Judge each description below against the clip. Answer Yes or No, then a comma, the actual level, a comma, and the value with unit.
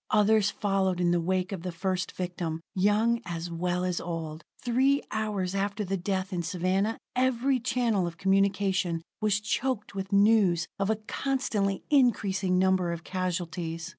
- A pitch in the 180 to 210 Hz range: Yes, high, 190 Hz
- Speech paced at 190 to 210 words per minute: No, average, 155 wpm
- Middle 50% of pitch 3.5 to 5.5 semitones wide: No, average, 3.1 semitones